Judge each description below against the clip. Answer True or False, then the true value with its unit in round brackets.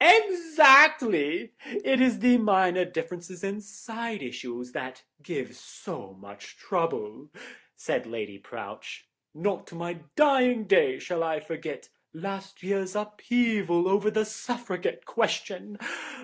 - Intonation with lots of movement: True (6.0 semitones)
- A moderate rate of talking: False (120 wpm)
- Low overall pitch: False (195 Hz)